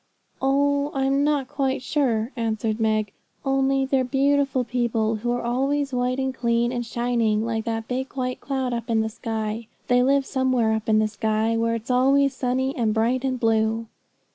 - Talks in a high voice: Yes, high, 245 Hz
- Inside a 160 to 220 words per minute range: Yes, average, 180 wpm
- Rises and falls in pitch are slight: No, average, 3.1 semitones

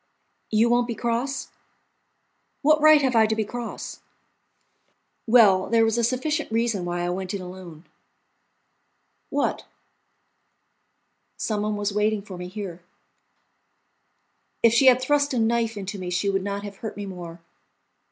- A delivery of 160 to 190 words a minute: No, average, 150 wpm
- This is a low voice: No, high, 215 Hz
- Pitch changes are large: No, average, 3.7 semitones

